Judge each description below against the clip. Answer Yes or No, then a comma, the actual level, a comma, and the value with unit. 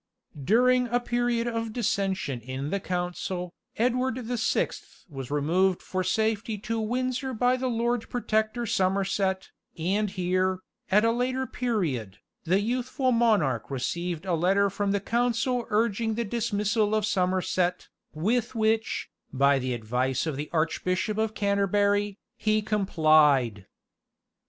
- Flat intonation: No, average, 4.7 semitones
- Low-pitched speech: No, high, 205 Hz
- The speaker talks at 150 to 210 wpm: No, slow, 135 wpm